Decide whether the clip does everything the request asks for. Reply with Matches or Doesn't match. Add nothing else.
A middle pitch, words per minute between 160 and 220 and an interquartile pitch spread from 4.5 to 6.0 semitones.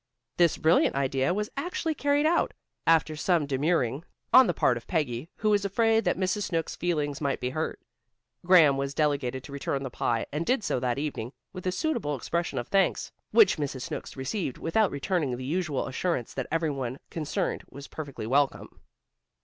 Matches